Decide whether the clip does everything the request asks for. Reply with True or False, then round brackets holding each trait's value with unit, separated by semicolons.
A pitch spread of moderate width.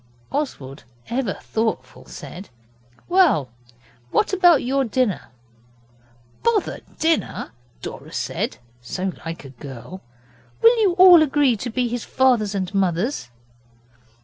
False (8.6 semitones)